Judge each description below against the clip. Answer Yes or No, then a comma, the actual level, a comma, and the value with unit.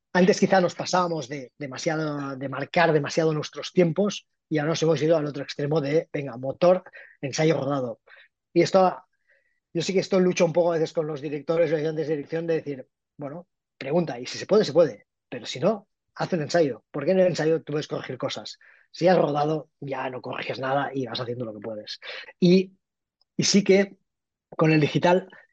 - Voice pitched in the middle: Yes, medium, 160 Hz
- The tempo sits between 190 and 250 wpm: Yes, average, 200 wpm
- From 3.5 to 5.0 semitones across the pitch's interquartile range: Yes, average, 3.8 semitones